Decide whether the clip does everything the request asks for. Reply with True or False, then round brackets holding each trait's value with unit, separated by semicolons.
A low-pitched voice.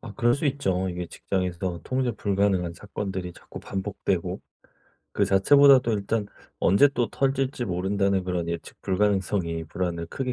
True (100 Hz)